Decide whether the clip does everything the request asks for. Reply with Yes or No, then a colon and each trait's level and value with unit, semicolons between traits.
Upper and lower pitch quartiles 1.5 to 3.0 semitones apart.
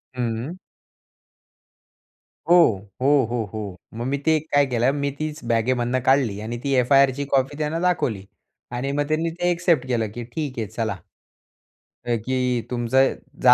No: average, 3.5 semitones